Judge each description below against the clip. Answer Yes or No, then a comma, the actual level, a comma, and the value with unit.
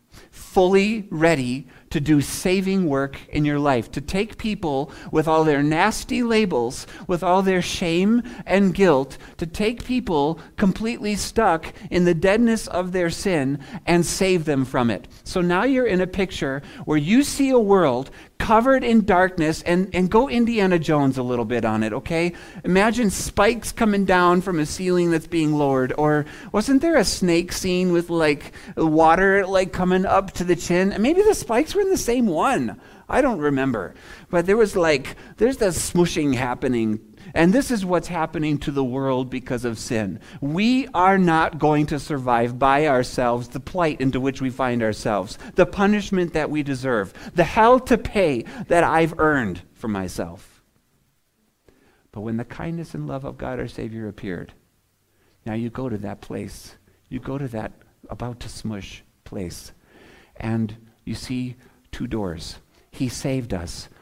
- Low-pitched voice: No, medium, 160 Hz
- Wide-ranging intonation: Yes, wide, 6.6 semitones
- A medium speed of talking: Yes, average, 170 wpm